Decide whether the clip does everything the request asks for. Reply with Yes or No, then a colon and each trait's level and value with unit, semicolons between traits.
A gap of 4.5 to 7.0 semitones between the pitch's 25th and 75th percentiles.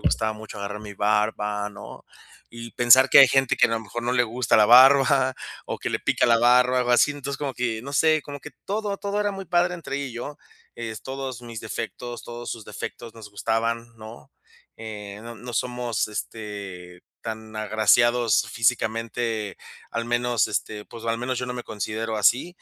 No: narrow, 2.6 semitones